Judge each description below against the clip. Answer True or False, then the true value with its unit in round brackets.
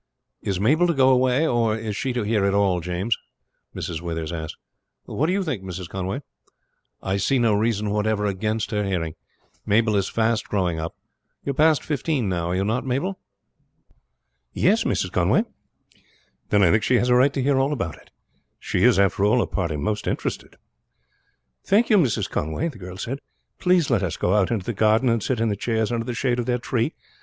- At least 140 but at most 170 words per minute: False (205 wpm)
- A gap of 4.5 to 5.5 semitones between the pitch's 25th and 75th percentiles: True (4.8 semitones)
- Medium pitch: False (110 Hz)